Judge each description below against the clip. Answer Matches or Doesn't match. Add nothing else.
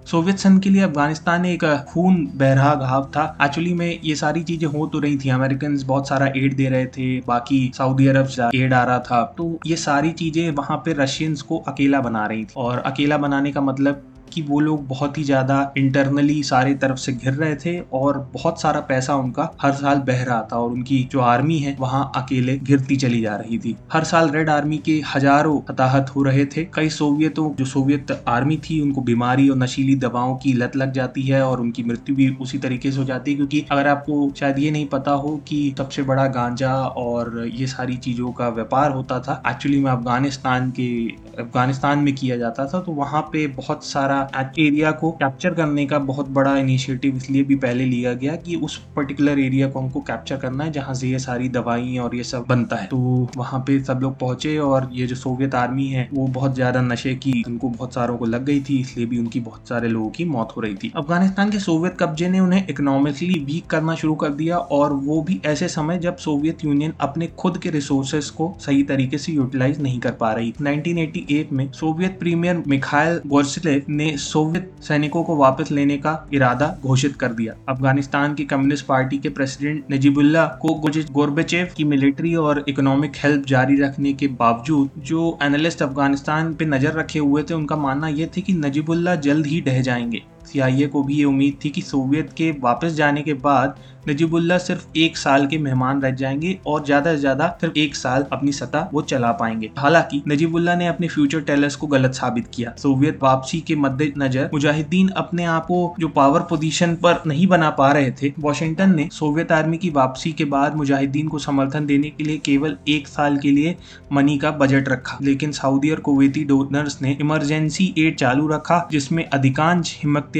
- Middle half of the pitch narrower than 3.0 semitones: Matches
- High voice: Doesn't match